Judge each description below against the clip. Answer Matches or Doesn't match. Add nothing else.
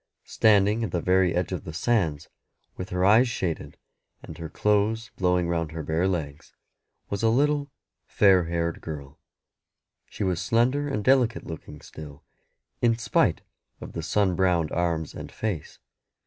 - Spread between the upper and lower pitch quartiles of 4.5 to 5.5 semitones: Matches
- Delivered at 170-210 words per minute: Doesn't match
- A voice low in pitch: Matches